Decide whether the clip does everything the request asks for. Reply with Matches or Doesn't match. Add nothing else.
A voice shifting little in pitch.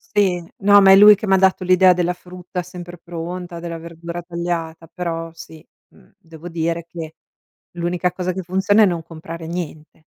Matches